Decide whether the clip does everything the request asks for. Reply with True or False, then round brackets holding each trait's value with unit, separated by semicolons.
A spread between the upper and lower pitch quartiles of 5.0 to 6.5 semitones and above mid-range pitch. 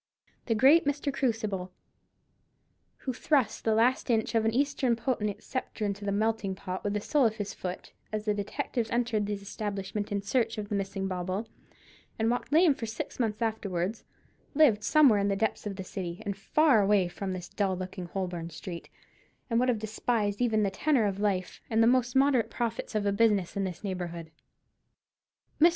False (3.3 semitones; 215 Hz)